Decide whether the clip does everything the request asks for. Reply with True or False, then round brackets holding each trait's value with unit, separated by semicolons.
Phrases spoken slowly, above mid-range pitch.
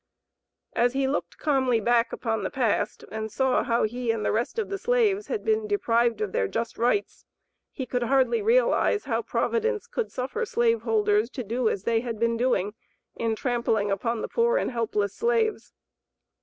False (185 wpm; 240 Hz)